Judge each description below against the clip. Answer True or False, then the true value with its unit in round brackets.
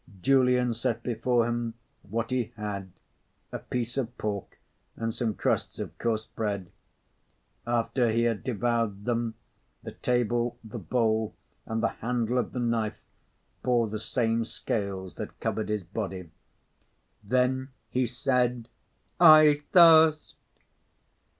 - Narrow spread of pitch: True (2.3 semitones)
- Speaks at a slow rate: True (125 wpm)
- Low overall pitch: True (115 Hz)